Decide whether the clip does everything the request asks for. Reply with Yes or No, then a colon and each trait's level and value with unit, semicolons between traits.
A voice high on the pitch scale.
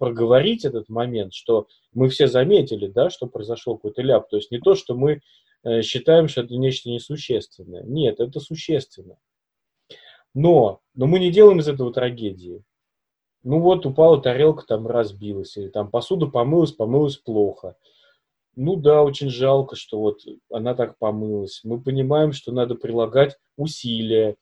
No: low, 125 Hz